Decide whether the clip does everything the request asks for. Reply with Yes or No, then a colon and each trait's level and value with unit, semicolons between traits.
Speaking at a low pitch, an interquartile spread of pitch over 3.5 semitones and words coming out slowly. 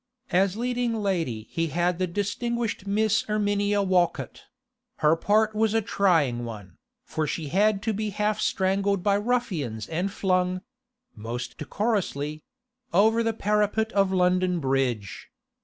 No: high, 200 Hz; average, 4.5 semitones; slow, 125 wpm